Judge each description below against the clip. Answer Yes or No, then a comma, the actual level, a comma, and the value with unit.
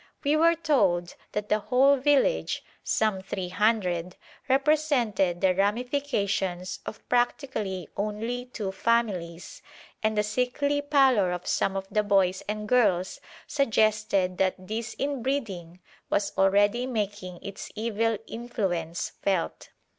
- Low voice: No, high, 210 Hz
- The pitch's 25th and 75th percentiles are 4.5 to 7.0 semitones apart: Yes, average, 4.8 semitones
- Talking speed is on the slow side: Yes, slow, 120 wpm